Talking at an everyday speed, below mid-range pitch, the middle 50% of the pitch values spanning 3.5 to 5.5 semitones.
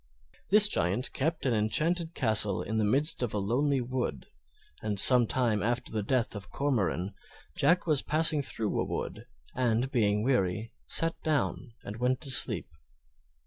Yes: average, 160 wpm; low, 125 Hz; average, 4.9 semitones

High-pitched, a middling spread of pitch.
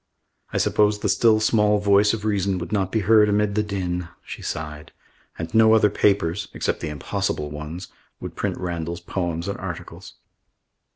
No: low, 100 Hz; average, 3.6 semitones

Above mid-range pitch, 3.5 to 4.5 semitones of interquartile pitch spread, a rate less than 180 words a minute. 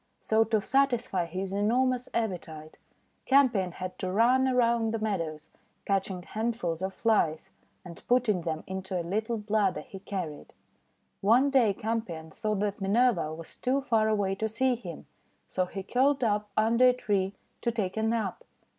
Yes: high, 210 Hz; average, 4.0 semitones; average, 165 wpm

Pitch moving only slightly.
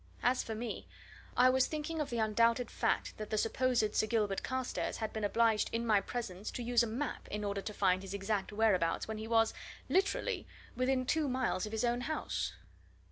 No: average, 3.0 semitones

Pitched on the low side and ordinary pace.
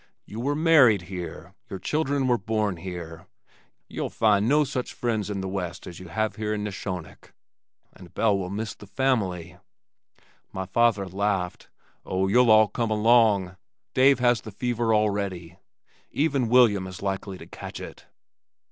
Yes: low, 105 Hz; average, 155 wpm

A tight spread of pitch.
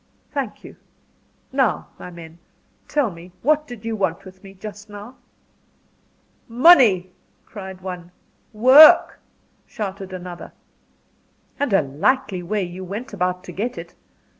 No: average, 4.7 semitones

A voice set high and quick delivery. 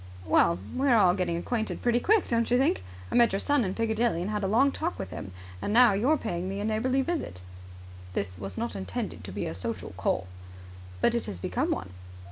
Yes: high, 215 Hz; fast, 225 wpm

